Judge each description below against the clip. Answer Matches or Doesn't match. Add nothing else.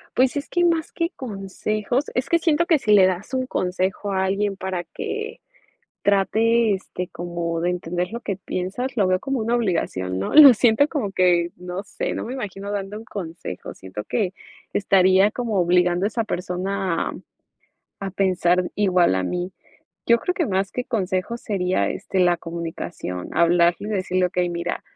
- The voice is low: Doesn't match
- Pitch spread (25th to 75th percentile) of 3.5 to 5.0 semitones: Matches